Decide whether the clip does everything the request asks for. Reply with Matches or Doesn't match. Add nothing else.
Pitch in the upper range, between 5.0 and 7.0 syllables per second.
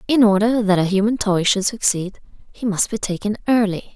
Matches